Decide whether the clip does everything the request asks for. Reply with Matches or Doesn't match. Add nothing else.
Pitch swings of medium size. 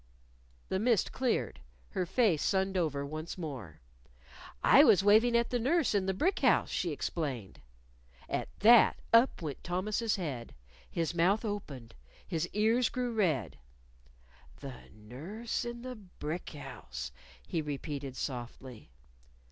Doesn't match